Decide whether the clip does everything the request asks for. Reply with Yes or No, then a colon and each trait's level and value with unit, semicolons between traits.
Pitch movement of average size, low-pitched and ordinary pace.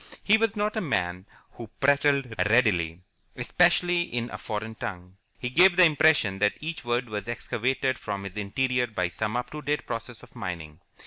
No: wide, 6.6 semitones; low, 120 Hz; average, 180 wpm